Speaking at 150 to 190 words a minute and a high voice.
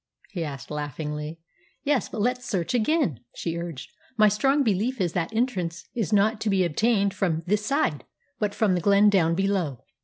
Yes: average, 180 wpm; high, 195 Hz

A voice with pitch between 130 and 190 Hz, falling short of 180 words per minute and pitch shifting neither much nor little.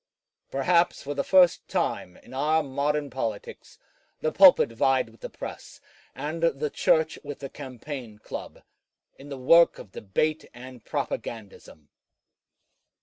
Yes: medium, 140 Hz; slow, 135 wpm; average, 3.9 semitones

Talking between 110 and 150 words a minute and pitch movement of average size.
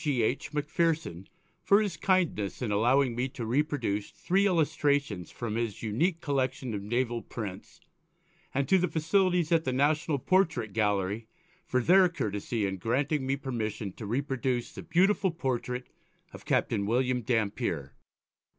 No: average, 145 wpm; wide, 6.1 semitones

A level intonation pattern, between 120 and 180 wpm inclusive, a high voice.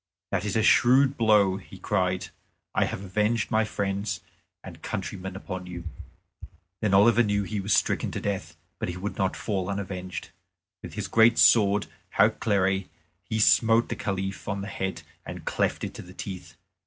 No: narrow, 2.2 semitones; average, 170 wpm; low, 100 Hz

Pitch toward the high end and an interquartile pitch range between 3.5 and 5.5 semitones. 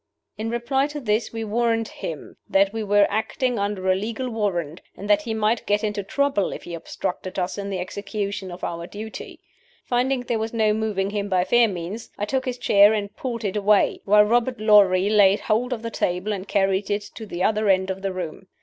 No: high, 210 Hz; average, 2.7 semitones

